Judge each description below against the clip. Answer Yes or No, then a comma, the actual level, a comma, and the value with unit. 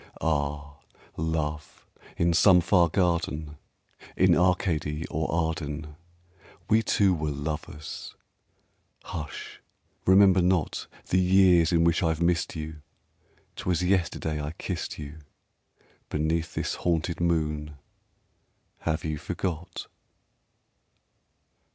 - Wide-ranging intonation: No, narrow, 2.5 semitones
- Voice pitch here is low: Yes, very low, 80 Hz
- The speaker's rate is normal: No, slow, 100 wpm